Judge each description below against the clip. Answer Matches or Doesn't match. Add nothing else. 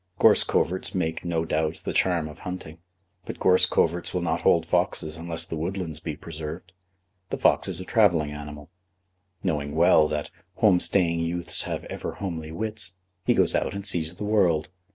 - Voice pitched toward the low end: Matches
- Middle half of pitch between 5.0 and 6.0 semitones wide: Doesn't match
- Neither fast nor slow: Matches